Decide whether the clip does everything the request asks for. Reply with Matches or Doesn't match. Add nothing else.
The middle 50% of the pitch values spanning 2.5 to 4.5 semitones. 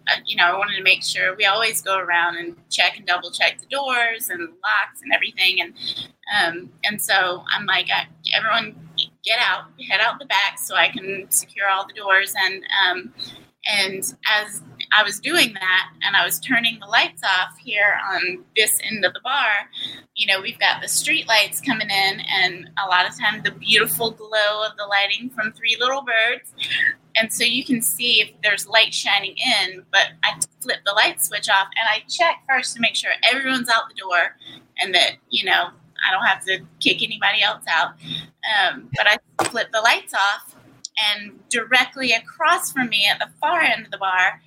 Matches